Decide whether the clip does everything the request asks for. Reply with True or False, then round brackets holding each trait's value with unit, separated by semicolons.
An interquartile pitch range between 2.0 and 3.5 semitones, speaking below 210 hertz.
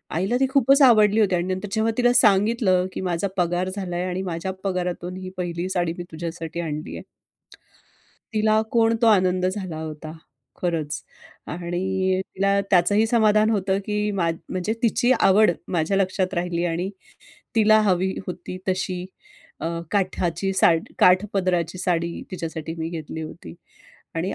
True (3.2 semitones; 185 Hz)